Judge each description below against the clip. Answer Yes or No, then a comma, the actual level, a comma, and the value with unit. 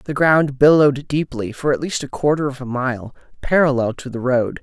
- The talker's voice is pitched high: No, low, 135 Hz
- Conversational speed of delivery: No, fast, 210 wpm